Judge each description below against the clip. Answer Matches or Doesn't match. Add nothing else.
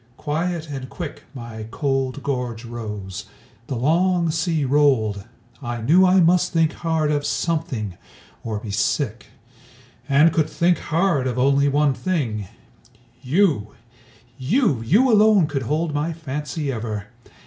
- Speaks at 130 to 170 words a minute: Matches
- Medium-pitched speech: Matches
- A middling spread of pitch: Doesn't match